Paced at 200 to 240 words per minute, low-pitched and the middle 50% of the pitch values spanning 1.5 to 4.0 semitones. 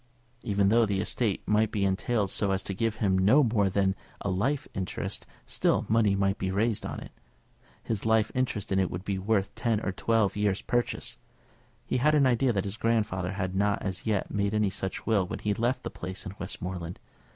Yes: fast, 205 wpm; low, 100 Hz; average, 2.8 semitones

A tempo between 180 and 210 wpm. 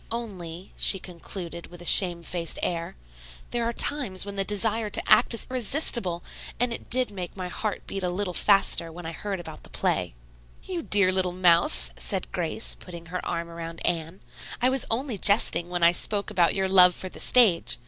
Yes: average, 200 wpm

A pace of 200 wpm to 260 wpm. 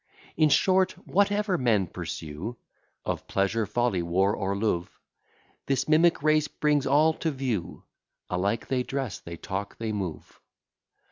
No: slow, 135 wpm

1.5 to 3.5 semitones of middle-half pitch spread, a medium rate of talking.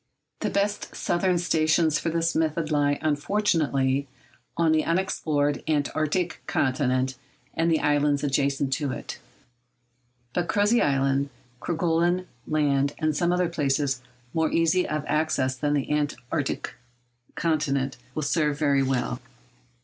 No: average, 3.0 semitones; slow, 125 wpm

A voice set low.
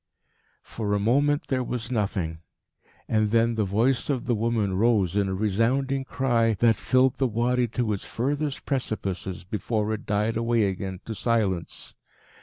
Yes: low, 115 Hz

